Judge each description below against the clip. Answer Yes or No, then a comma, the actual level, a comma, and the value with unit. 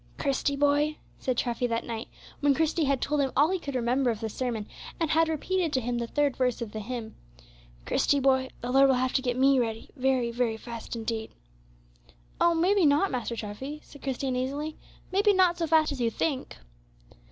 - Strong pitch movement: No, average, 3.8 semitones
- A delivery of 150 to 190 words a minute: No, fast, 205 wpm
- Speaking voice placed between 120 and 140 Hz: No, very high, 265 Hz